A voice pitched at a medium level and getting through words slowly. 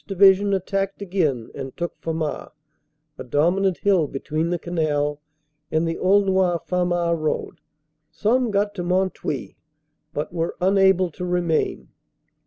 Yes: medium, 175 Hz; slow, 130 wpm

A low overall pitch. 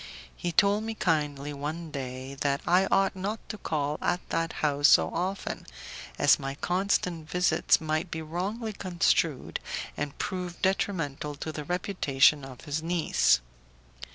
No: medium, 160 Hz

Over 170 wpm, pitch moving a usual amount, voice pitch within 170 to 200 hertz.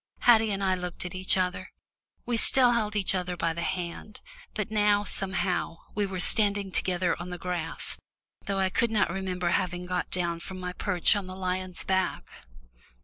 No: average, 185 wpm; narrow, 2.2 semitones; medium, 185 Hz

